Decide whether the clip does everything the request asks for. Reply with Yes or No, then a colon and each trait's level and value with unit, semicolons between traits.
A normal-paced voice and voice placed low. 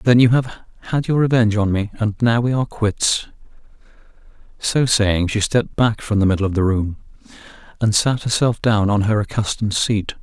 Yes: average, 190 wpm; low, 110 Hz